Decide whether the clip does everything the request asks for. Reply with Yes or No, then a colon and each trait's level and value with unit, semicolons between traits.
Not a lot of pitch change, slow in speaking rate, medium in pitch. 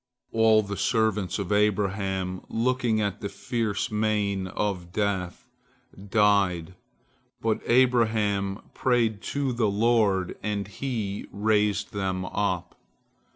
No: narrow, 2.2 semitones; slow, 110 wpm; low, 105 Hz